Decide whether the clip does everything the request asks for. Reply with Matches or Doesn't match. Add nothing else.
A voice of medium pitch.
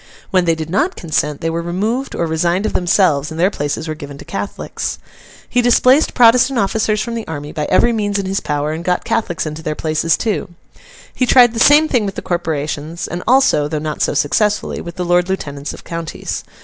Matches